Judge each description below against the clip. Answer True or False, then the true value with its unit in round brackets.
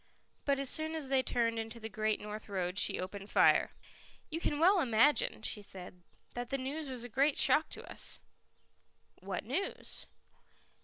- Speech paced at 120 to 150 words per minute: False (170 wpm)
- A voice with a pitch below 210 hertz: False (245 Hz)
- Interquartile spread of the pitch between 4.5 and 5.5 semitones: True (5.0 semitones)